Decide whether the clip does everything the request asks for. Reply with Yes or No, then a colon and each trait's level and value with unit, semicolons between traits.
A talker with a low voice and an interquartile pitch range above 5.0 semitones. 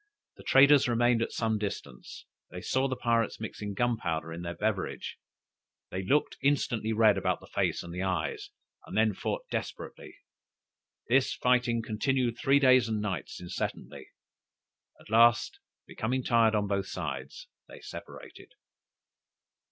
No: low, 110 Hz; average, 4.1 semitones